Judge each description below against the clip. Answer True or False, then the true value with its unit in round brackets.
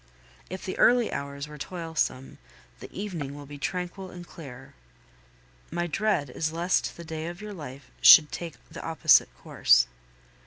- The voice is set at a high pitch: False (165 Hz)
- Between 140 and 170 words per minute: True (155 wpm)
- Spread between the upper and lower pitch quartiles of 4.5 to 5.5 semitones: False (3.9 semitones)